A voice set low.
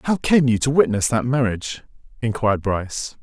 Yes: low, 120 Hz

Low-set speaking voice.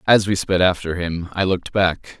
Yes: very low, 90 Hz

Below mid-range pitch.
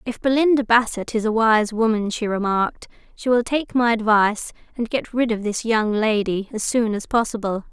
No: high, 225 Hz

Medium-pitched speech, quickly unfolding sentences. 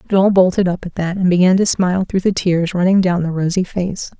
Yes: medium, 180 Hz; fast, 245 wpm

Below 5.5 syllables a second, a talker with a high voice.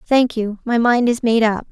Yes: 4.7 syllables/s; high, 235 Hz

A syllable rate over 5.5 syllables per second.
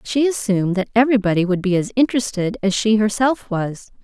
Yes: 5.9 syllables/s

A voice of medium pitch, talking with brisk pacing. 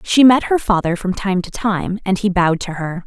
No: high, 195 Hz; fast, 255 wpm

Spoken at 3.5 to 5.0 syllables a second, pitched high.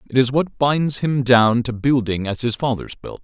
No: 4.7 syllables/s; low, 125 Hz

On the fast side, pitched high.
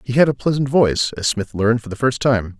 No: fast, 275 wpm; low, 120 Hz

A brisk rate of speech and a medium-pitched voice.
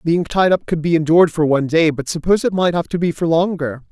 Yes: fast, 275 wpm; medium, 165 Hz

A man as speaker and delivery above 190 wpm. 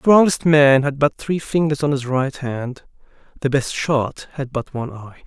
Yes: male; fast, 205 wpm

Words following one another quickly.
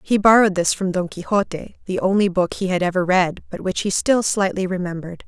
Yes: fast, 215 wpm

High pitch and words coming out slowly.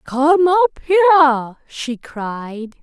Yes: very high, 290 Hz; slow, 105 wpm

